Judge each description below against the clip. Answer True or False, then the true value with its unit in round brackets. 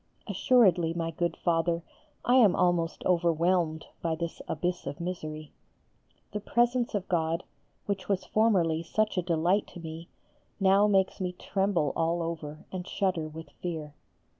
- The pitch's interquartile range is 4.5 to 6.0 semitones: False (2.8 semitones)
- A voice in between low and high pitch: True (175 Hz)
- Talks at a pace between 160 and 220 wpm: False (145 wpm)